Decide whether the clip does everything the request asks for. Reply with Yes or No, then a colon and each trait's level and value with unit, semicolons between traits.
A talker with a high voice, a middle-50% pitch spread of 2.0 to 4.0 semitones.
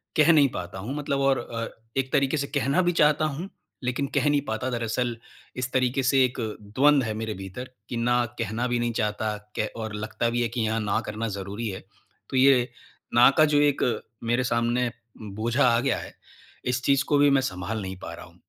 No: low, 120 Hz; average, 3.6 semitones